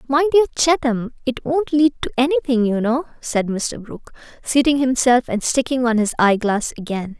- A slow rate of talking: No, average, 185 wpm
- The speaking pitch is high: Yes, very high, 250 Hz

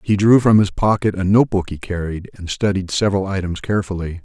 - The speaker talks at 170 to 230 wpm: Yes, average, 200 wpm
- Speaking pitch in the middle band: No, very low, 95 Hz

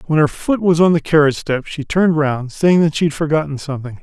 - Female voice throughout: No, male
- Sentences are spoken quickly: Yes, fast, 255 wpm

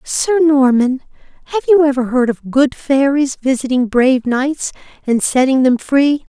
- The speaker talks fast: No, average, 150 wpm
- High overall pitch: Yes, very high, 270 Hz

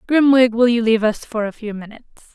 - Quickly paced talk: Yes, fast, 230 wpm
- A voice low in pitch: No, high, 230 Hz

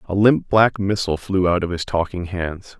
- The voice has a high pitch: No, very low, 95 Hz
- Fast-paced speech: Yes, fast, 215 wpm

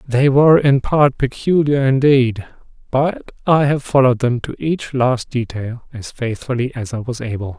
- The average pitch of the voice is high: No, low, 130 Hz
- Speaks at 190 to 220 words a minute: No, average, 165 wpm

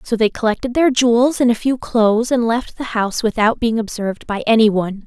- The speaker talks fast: Yes, fast, 215 wpm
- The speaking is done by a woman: Yes, female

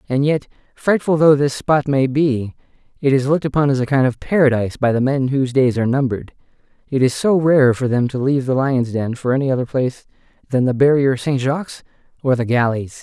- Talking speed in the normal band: No, fast, 215 wpm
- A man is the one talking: Yes, male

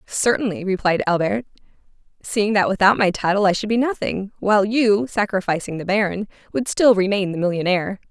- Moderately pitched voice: No, high, 200 Hz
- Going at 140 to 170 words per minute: Yes, average, 165 wpm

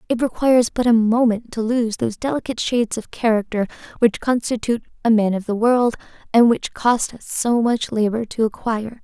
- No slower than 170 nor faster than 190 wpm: Yes, average, 185 wpm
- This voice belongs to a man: No, female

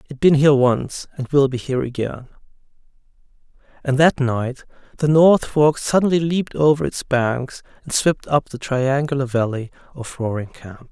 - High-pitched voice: No, low, 135 Hz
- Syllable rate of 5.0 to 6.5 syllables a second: No, 4.8 syllables/s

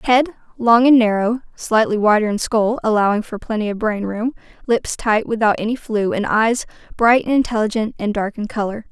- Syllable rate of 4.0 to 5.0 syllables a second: No, 5.2 syllables/s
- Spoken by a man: No, female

